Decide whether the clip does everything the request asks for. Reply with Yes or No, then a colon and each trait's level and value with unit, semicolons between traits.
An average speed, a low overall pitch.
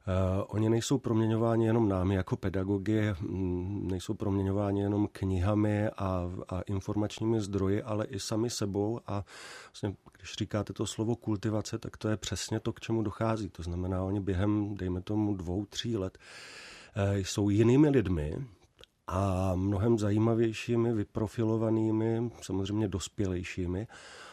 Yes: average, 130 wpm; low, 105 Hz